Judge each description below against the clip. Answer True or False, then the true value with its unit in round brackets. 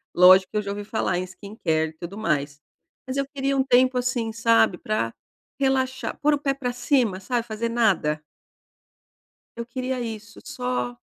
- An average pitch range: False (5.8 semitones)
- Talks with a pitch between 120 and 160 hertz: False (225 Hz)